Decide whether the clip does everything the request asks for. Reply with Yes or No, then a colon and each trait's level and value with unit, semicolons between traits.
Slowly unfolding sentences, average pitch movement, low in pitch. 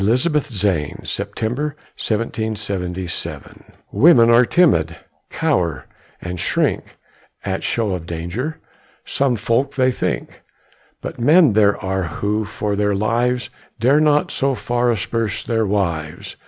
Yes: slow, 115 wpm; average, 4.7 semitones; low, 110 Hz